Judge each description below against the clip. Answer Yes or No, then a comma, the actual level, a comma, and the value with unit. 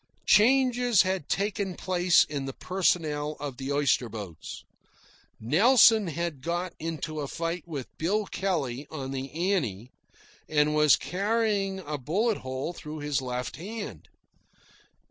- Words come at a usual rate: No, slow, 130 wpm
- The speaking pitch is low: No, medium, 160 Hz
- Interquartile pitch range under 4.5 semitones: No, wide, 5.6 semitones